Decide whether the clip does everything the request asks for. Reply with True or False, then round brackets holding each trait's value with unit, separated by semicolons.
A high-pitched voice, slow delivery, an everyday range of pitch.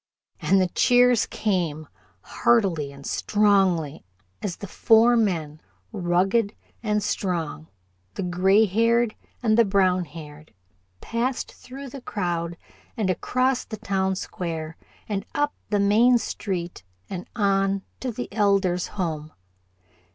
True (195 Hz; 120 wpm; 4.2 semitones)